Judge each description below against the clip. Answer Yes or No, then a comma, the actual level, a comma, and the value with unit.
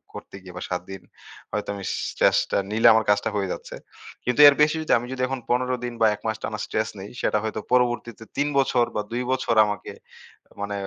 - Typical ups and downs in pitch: Yes, average, 3.3 semitones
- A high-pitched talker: No, low, 115 Hz